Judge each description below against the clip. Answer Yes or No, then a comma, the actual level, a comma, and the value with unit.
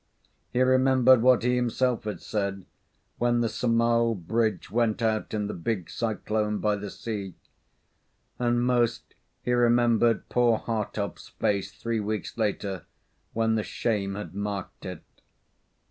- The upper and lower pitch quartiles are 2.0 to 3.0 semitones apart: Yes, narrow, 2.5 semitones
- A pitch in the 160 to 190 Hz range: No, low, 115 Hz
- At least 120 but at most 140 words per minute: Yes, slow, 135 wpm